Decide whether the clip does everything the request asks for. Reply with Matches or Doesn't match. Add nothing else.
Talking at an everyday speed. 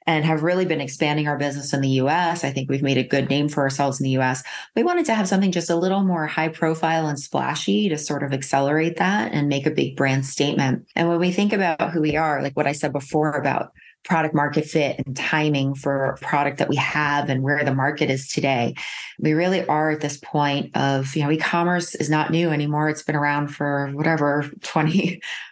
Doesn't match